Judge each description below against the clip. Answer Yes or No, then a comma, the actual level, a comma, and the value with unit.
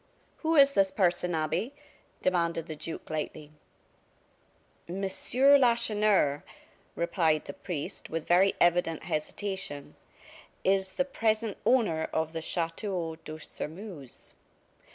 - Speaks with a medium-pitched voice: Yes, medium, 175 Hz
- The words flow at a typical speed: No, slow, 110 wpm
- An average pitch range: Yes, average, 4.6 semitones